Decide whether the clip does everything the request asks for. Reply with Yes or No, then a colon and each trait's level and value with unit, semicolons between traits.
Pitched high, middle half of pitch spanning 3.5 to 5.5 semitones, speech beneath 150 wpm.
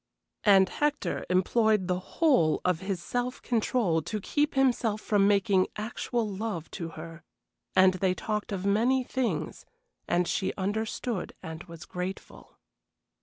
Yes: high, 200 Hz; average, 4.2 semitones; slow, 135 wpm